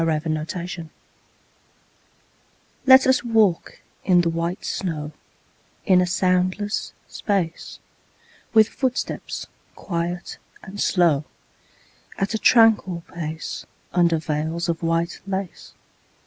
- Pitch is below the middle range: No, medium, 175 Hz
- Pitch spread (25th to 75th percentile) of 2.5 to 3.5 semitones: Yes, average, 3.1 semitones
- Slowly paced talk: Yes, slow, 100 wpm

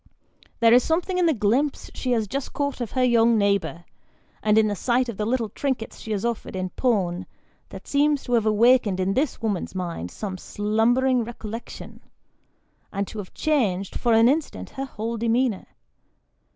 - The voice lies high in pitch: Yes, high, 230 Hz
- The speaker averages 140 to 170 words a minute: No, average, 180 wpm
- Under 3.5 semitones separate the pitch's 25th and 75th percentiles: No, average, 4.0 semitones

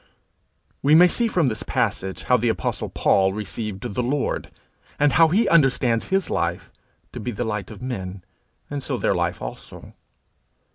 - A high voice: No, low, 120 Hz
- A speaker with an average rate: Yes, average, 170 wpm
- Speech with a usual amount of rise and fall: No, wide, 6.7 semitones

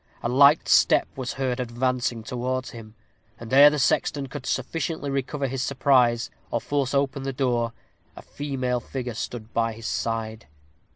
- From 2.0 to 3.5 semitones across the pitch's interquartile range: Yes, narrow, 2.6 semitones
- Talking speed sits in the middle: Yes, average, 160 wpm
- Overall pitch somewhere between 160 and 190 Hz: No, low, 130 Hz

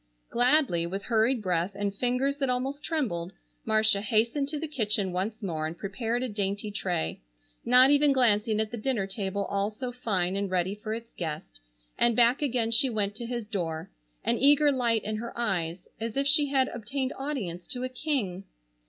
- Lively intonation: No, average, 4.5 semitones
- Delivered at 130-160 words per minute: No, average, 190 wpm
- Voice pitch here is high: Yes, high, 220 Hz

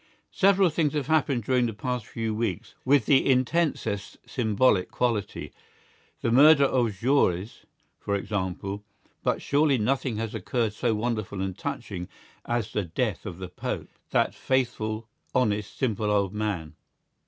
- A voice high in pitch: No, low, 115 Hz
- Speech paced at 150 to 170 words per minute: No, average, 140 wpm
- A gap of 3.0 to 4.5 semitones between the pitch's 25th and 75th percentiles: Yes, average, 4.2 semitones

